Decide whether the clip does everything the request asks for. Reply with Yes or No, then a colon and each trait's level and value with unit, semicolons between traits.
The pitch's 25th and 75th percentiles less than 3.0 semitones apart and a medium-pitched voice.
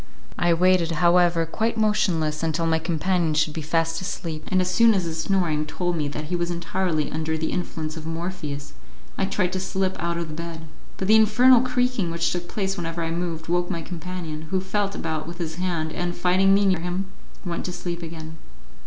Yes: narrow, 2.5 semitones; medium, 170 Hz